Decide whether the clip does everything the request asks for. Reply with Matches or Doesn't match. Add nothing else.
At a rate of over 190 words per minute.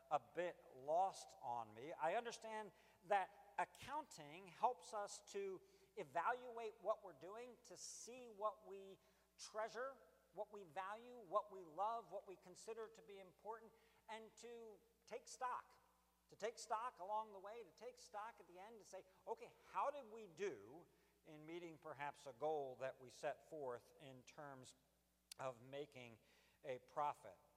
Doesn't match